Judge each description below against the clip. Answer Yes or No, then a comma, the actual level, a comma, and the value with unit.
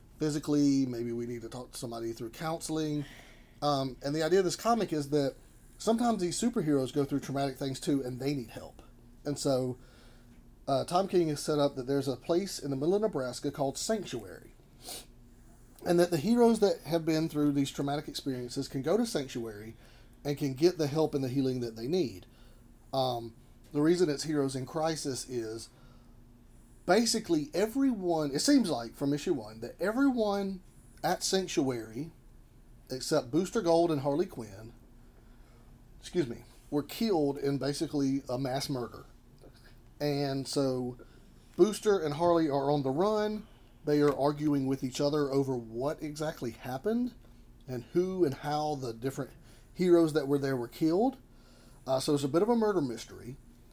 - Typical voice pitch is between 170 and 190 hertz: No, medium, 140 Hz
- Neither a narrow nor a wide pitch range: Yes, average, 4.4 semitones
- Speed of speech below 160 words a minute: No, average, 165 wpm